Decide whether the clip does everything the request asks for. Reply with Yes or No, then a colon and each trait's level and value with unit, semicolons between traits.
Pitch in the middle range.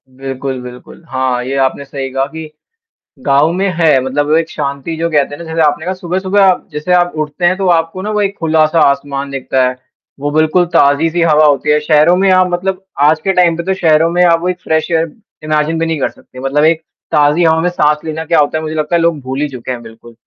Yes: medium, 155 Hz